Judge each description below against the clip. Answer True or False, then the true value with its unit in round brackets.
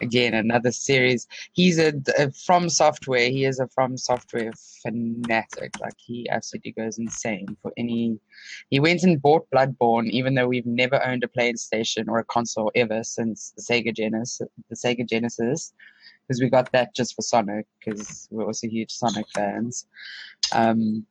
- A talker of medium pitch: False (120 Hz)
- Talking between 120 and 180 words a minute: True (165 wpm)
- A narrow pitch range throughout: True (2.1 semitones)